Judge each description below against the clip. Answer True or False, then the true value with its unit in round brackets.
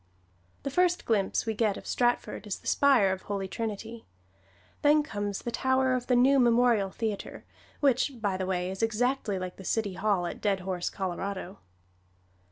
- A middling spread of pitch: True (4.4 semitones)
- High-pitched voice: True (215 Hz)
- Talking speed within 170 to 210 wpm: True (175 wpm)